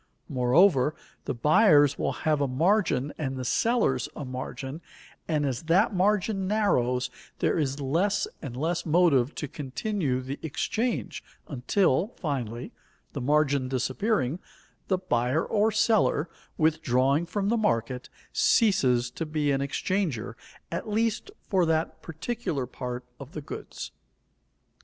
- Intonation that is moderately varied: No, wide, 6.7 semitones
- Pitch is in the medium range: Yes, medium, 150 Hz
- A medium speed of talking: No, slow, 130 wpm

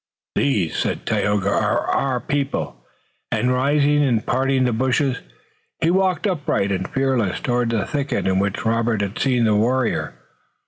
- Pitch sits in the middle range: No, low, 125 Hz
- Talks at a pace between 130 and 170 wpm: Yes, average, 150 wpm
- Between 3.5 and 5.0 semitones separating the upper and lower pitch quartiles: Yes, average, 4.4 semitones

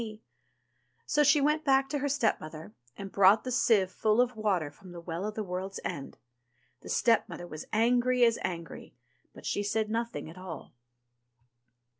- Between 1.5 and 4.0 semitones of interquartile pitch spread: No, average, 5.1 semitones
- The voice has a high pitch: Yes, high, 215 Hz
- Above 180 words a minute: No, average, 170 wpm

